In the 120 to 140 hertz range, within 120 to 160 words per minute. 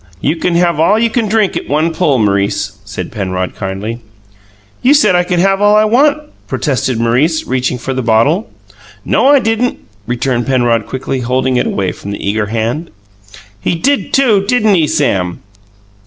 No: low, 135 Hz; average, 175 wpm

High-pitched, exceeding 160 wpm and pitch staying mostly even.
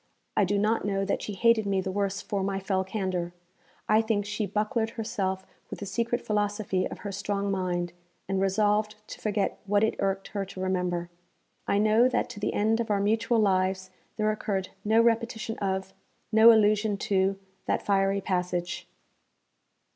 Yes: high, 200 Hz; average, 175 wpm; narrow, 2.1 semitones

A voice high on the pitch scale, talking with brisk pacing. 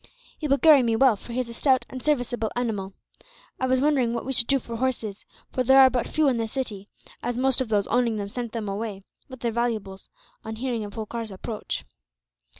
Yes: high, 235 Hz; fast, 225 wpm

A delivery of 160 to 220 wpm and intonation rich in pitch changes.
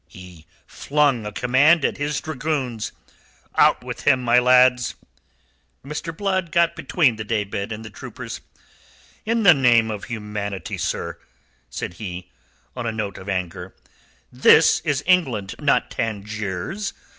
No: average, 140 wpm; wide, 6.4 semitones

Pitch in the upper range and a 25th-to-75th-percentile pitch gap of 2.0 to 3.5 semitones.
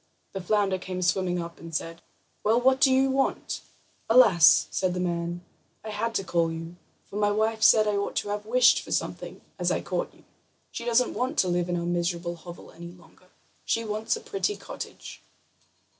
No: high, 195 Hz; average, 4.5 semitones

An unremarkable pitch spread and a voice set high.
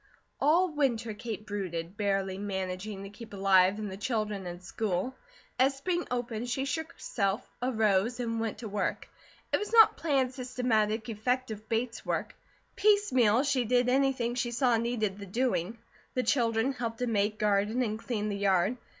Yes: average, 3.7 semitones; high, 225 Hz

